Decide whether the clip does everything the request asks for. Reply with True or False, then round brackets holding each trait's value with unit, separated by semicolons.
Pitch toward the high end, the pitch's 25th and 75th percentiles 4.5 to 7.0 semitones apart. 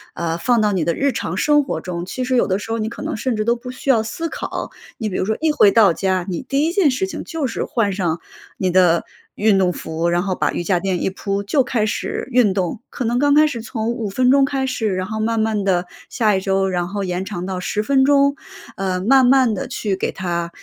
True (210 Hz; 5.3 semitones)